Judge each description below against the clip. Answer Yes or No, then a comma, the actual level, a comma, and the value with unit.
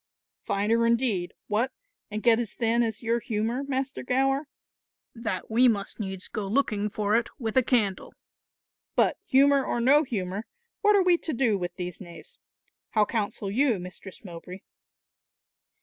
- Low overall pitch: No, high, 225 Hz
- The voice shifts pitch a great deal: No, average, 4.4 semitones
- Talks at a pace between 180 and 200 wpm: No, average, 155 wpm